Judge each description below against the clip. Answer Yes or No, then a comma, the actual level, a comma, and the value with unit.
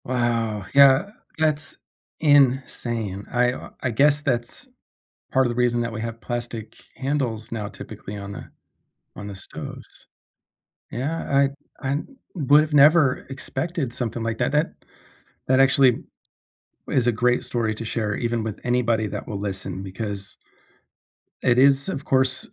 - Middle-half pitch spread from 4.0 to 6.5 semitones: No, average, 3.4 semitones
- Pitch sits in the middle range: No, low, 125 Hz